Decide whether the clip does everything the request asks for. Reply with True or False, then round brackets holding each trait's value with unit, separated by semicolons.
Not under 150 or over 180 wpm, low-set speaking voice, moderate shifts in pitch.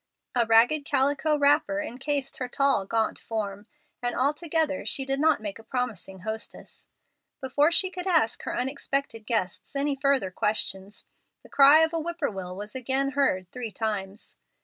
False (155 wpm; 265 Hz; 4.9 semitones)